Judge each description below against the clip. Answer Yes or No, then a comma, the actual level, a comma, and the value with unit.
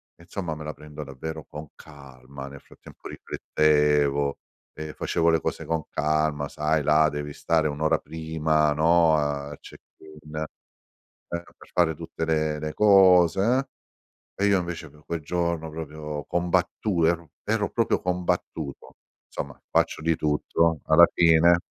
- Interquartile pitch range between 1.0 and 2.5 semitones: Yes, narrow, 2.2 semitones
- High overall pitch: No, very low, 80 Hz